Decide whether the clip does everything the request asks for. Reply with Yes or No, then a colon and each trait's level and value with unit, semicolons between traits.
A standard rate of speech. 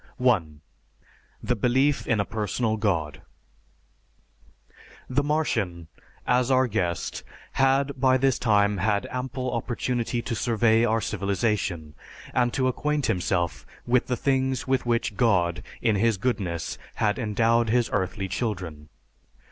No: slow, 125 wpm